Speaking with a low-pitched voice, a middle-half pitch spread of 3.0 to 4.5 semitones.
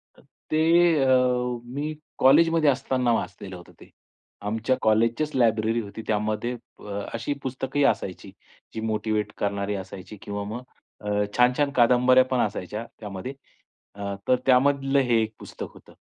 Yes: low, 120 Hz; average, 3.9 semitones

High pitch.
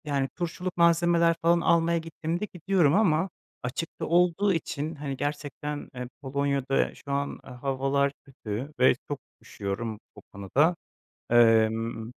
No: medium, 145 Hz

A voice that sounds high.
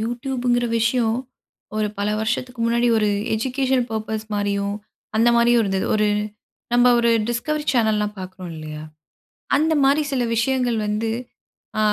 Yes: high, 230 Hz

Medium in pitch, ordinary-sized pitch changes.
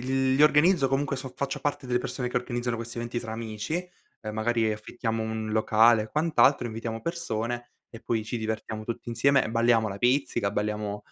No: low, 115 Hz; average, 3.0 semitones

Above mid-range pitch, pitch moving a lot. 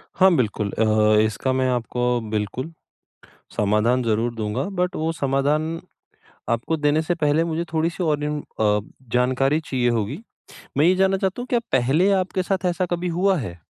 No: medium, 145 Hz; wide, 6.1 semitones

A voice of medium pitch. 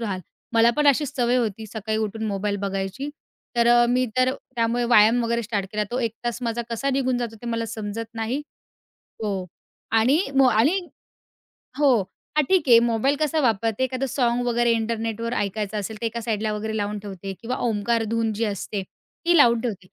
No: high, 230 Hz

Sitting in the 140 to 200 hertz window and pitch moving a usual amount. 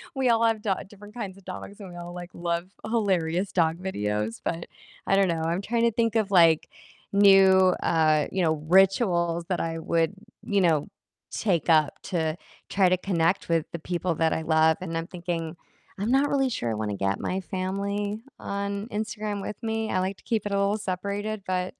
Yes: medium, 185 Hz; average, 3.5 semitones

